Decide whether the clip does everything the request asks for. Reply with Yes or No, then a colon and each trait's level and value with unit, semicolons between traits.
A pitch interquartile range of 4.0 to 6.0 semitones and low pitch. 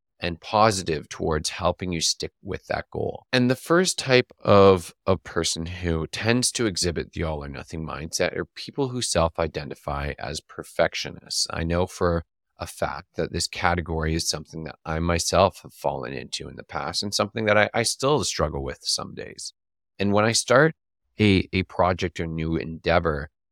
Yes: average, 4.4 semitones; very low, 85 Hz